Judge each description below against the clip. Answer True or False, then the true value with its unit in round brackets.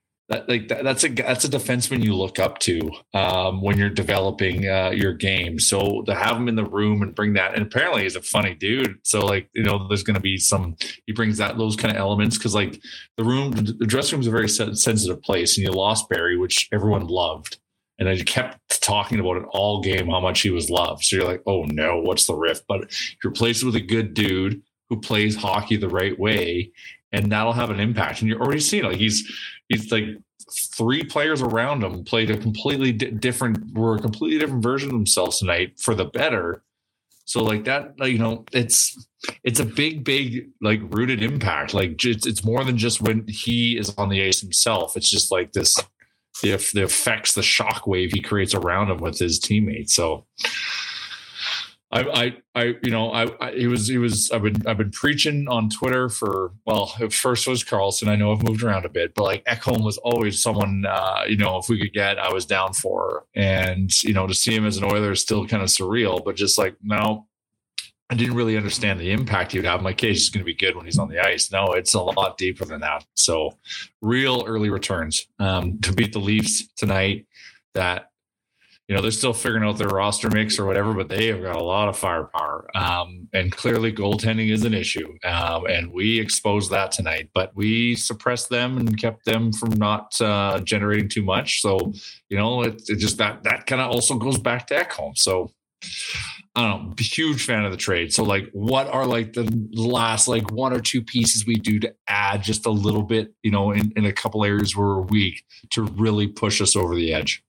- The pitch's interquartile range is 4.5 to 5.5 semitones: False (2.7 semitones)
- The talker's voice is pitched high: False (110 Hz)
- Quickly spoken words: True (220 wpm)